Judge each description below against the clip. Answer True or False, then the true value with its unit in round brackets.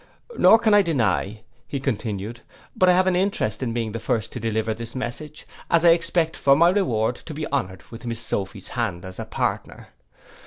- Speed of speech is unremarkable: True (195 wpm)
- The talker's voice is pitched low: True (120 Hz)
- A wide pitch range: True (7.2 semitones)